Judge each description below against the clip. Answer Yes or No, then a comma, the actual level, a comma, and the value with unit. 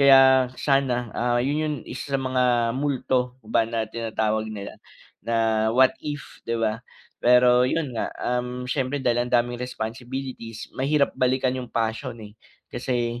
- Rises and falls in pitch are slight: Yes, narrow, 2.2 semitones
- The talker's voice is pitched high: No, low, 125 Hz